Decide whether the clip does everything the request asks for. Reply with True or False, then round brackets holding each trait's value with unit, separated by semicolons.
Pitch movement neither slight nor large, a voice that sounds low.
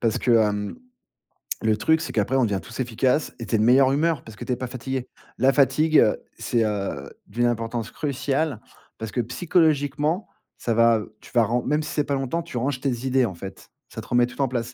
True (3.4 semitones; 125 Hz)